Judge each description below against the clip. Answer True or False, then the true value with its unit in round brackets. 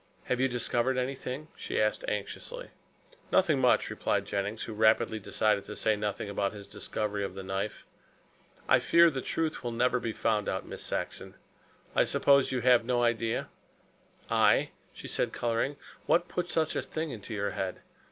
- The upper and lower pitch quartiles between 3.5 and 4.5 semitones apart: True (4.0 semitones)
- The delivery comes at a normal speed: True (170 wpm)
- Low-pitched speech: True (120 Hz)